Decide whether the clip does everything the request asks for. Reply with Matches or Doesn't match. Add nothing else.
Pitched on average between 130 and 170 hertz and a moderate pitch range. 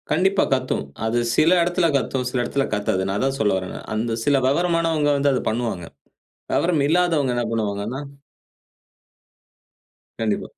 Doesn't match